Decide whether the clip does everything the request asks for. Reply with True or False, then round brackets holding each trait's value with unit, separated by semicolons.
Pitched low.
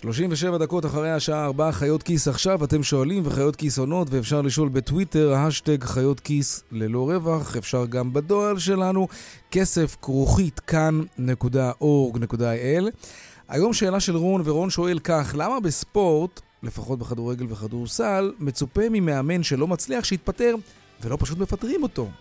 False (150 Hz)